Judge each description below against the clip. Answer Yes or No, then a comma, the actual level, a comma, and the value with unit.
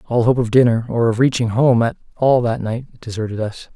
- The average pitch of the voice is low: Yes, low, 120 Hz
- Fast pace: Yes, fast, 225 wpm